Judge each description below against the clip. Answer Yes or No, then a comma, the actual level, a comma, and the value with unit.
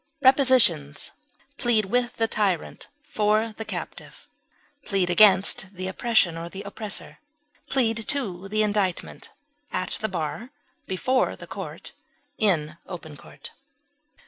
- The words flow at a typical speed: No, slow, 120 wpm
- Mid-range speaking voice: No, high, 205 Hz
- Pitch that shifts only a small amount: No, average, 3.9 semitones